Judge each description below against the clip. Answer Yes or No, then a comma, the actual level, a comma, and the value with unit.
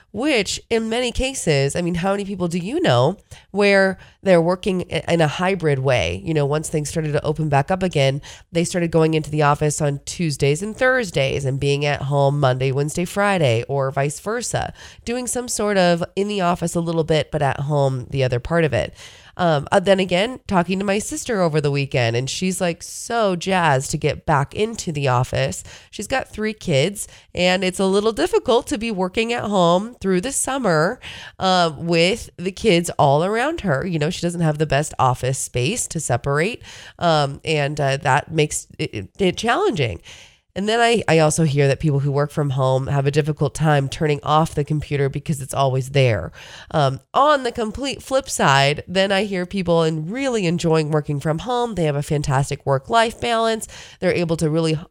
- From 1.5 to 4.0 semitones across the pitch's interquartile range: No, average, 5.3 semitones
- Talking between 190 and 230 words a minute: Yes, average, 200 wpm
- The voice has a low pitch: No, medium, 160 Hz